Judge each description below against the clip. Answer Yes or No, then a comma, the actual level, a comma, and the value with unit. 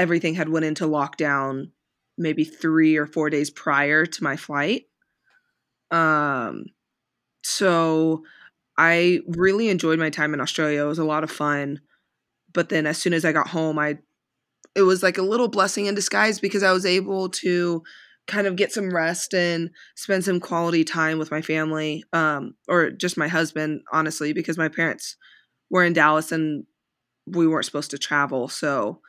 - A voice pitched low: No, medium, 160 Hz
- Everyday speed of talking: Yes, average, 170 wpm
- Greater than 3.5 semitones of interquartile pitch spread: No, average, 2.9 semitones